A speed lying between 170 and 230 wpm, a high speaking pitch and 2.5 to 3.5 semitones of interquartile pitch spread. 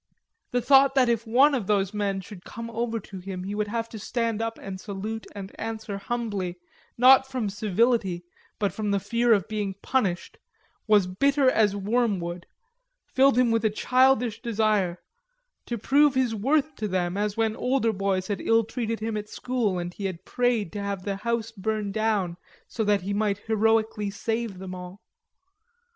Yes: average, 180 wpm; high, 215 Hz; average, 3.0 semitones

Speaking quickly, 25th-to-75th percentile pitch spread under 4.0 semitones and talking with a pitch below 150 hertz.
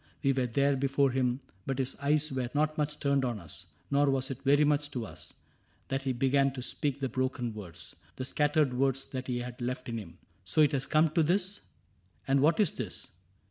Yes: fast, 220 wpm; narrow, 2.4 semitones; low, 135 Hz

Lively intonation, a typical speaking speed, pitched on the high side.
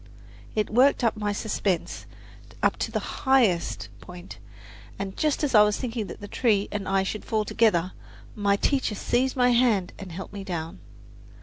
No: average, 3.8 semitones; average, 165 wpm; high, 210 Hz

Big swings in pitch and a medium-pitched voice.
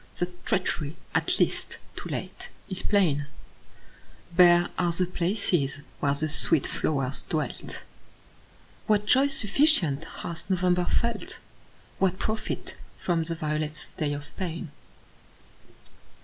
No: average, 3.7 semitones; medium, 175 Hz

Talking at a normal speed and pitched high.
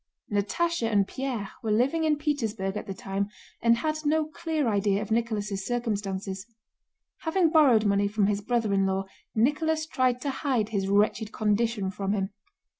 Yes: average, 165 wpm; high, 220 Hz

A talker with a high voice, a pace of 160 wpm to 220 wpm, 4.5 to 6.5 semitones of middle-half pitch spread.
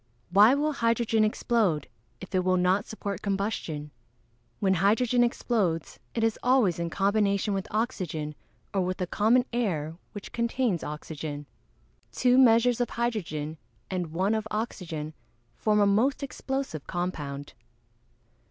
No: high, 200 Hz; slow, 135 wpm; average, 5.3 semitones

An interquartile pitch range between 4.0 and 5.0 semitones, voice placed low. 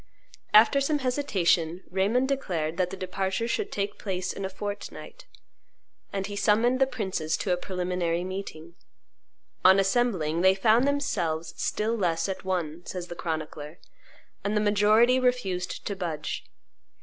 No: average, 4.3 semitones; high, 190 Hz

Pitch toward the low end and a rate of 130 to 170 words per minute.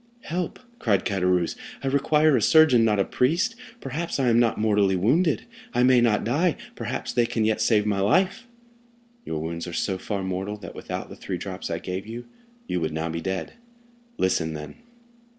No: low, 110 Hz; average, 185 wpm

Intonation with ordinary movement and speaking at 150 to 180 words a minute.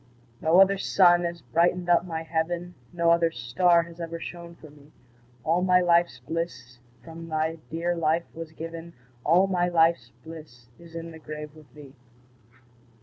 No: narrow, 1.5 semitones; average, 165 wpm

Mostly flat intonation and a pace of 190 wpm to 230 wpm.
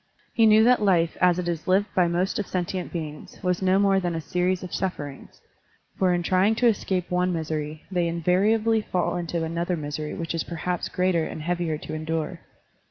Yes: narrow, 2.3 semitones; average, 195 wpm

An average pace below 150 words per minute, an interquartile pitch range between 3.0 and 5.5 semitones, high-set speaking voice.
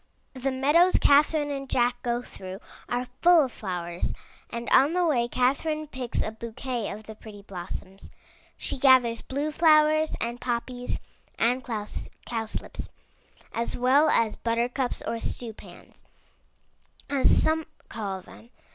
Yes: slow, 135 wpm; average, 3.8 semitones; high, 245 Hz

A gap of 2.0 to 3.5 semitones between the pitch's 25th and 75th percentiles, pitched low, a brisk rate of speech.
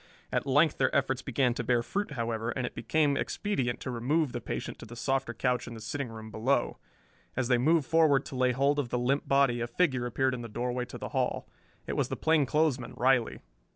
Yes: average, 2.8 semitones; low, 130 Hz; fast, 220 wpm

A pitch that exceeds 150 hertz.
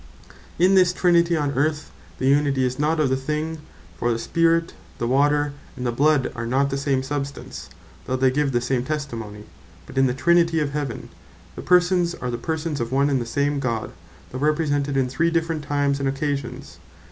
No: medium, 140 Hz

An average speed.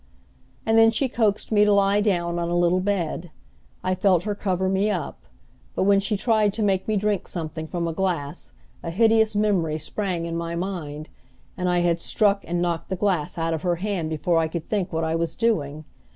No: fast, 210 wpm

